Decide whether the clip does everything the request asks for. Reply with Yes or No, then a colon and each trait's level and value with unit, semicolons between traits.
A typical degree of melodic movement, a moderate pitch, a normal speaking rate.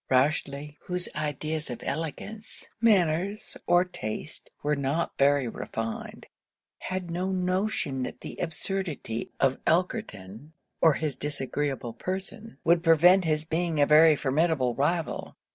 No: average, 4.3 semitones; medium, 155 Hz; slow, 125 wpm